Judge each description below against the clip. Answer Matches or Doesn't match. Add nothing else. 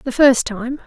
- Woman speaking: Matches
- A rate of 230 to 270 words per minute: Doesn't match